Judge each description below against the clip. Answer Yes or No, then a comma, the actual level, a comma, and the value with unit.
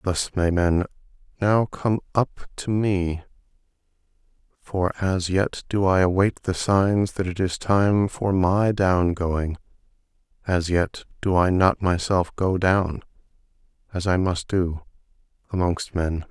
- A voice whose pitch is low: Yes, very low, 95 Hz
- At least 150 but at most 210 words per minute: No, average, 140 wpm